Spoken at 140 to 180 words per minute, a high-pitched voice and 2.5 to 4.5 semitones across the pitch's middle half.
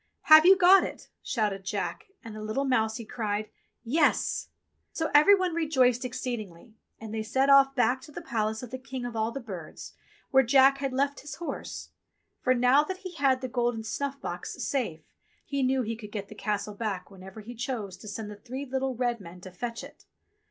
No: average, 200 wpm; high, 245 Hz; average, 4.2 semitones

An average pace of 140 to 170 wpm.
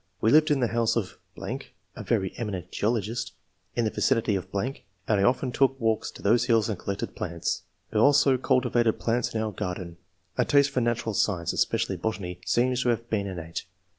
No: average, 195 wpm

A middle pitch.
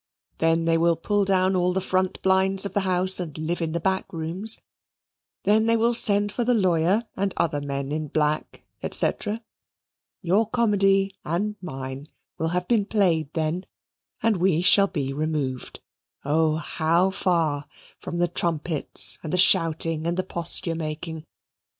Yes: medium, 175 Hz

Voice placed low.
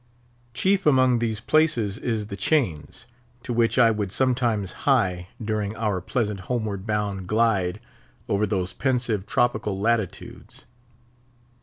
Yes: low, 110 Hz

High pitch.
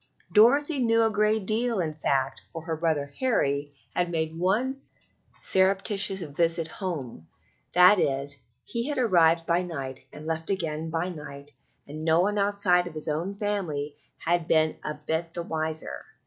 No: medium, 170 Hz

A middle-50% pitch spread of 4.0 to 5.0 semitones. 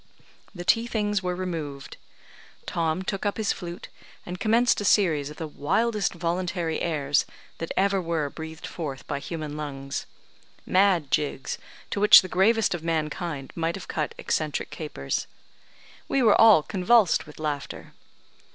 Yes: average, 4.4 semitones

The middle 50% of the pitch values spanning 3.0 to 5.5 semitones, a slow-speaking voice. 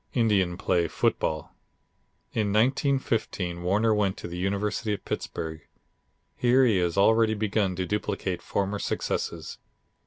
Yes: average, 3.6 semitones; slow, 125 wpm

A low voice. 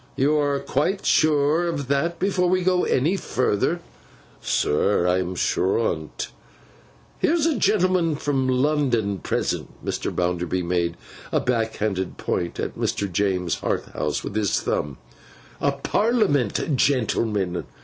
Yes: low, 130 Hz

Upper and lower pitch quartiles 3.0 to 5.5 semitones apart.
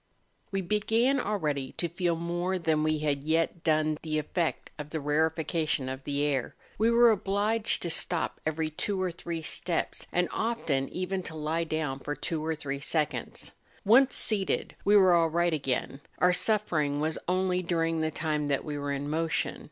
Yes: average, 3.3 semitones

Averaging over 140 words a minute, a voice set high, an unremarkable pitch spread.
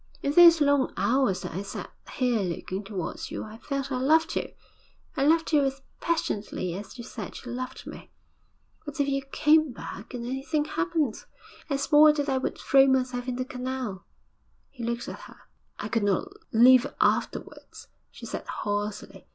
Yes: average, 175 wpm; very high, 260 Hz; average, 3.8 semitones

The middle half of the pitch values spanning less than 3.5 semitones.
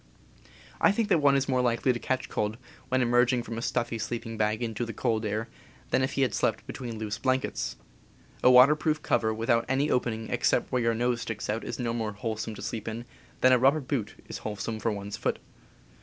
Yes: narrow, 2.6 semitones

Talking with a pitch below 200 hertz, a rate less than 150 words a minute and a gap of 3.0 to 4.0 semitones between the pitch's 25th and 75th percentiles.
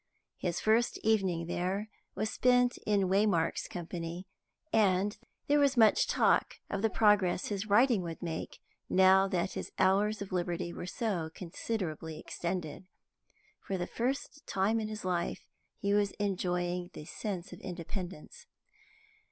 Yes: high, 190 Hz; average, 140 wpm; average, 3.4 semitones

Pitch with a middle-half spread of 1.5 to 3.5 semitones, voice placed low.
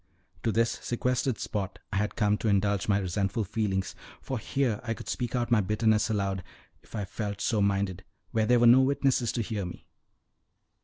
Yes: average, 2.9 semitones; low, 105 Hz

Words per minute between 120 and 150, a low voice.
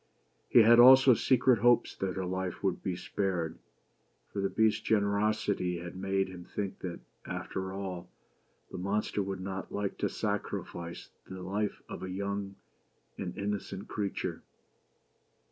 Yes: average, 145 wpm; very low, 95 Hz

